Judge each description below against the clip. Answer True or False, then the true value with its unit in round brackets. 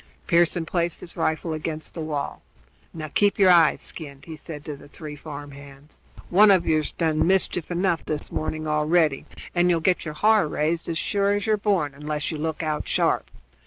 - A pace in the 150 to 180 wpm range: False (195 wpm)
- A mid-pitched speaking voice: True (160 Hz)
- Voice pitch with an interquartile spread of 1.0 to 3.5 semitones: True (2.6 semitones)